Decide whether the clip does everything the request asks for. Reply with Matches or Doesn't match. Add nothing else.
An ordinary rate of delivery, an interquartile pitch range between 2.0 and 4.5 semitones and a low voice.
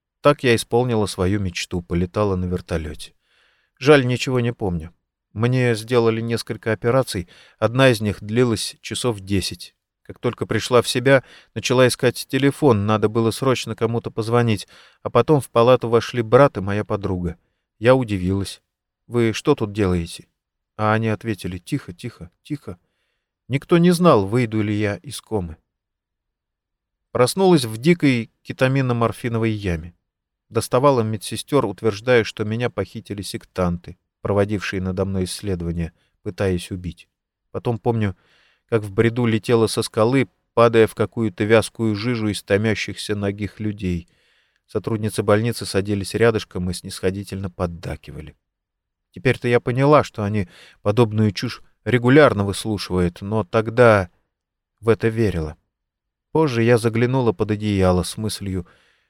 Matches